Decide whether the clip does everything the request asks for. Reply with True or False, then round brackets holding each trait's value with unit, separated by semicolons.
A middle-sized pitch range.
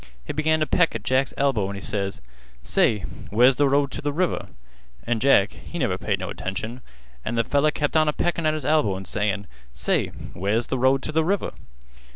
False (6.8 semitones)